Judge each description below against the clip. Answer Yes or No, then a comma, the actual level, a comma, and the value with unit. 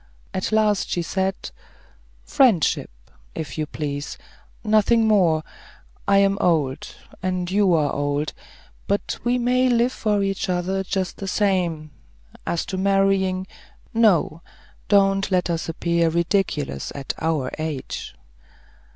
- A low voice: No, medium, 185 Hz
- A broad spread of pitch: No, average, 3.7 semitones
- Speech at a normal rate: No, slow, 125 wpm